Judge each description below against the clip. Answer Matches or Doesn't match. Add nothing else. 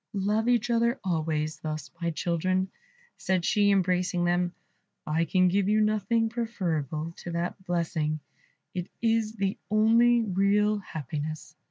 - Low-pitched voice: Doesn't match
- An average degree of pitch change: Matches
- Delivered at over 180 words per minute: Doesn't match